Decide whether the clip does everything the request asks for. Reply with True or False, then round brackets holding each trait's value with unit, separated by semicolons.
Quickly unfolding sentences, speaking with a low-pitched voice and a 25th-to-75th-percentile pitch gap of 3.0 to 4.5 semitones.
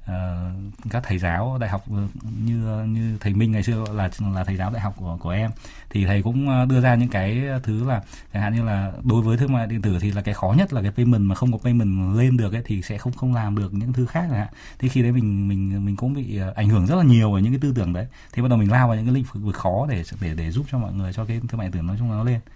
True (300 wpm; 110 Hz; 3.5 semitones)